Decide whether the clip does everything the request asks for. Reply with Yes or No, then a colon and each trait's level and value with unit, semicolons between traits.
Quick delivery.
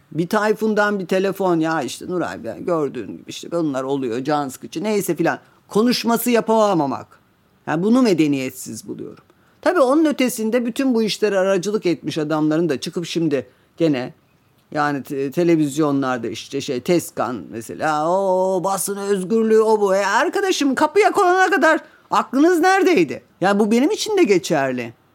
Yes: fast, 145 wpm